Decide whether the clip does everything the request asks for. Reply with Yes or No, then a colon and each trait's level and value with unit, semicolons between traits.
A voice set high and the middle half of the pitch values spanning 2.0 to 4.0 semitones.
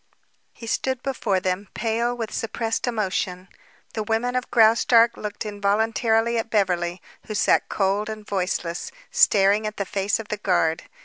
Yes: high, 215 Hz; narrow, 2.6 semitones